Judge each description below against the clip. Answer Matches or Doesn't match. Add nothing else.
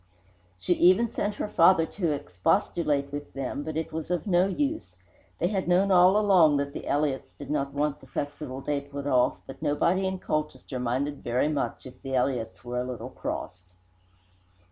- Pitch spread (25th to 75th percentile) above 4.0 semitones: Matches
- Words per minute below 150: Doesn't match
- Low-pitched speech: Doesn't match